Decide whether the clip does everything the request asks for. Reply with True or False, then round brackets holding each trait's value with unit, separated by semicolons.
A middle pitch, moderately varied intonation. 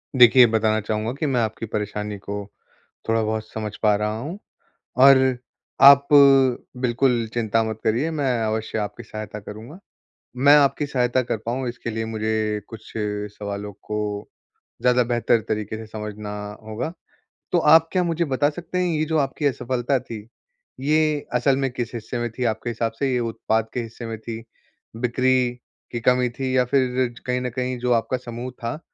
False (120 Hz; 3.2 semitones)